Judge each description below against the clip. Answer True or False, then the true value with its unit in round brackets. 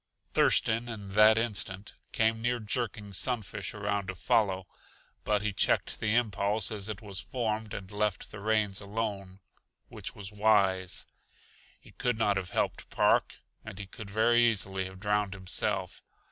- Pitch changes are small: True (2.2 semitones)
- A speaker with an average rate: True (155 wpm)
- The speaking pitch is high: False (105 Hz)